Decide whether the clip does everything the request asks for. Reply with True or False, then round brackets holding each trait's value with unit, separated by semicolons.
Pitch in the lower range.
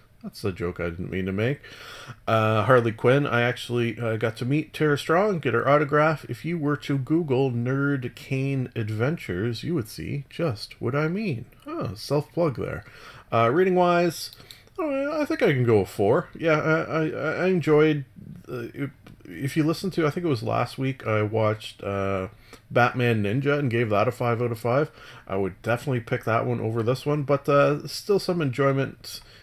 True (130 Hz)